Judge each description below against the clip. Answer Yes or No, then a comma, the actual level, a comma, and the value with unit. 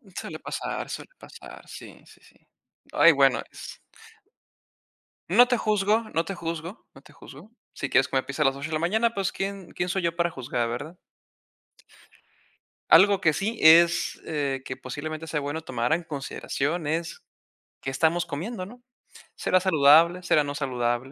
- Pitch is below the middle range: No, medium, 160 Hz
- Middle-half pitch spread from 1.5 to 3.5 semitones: No, average, 4.5 semitones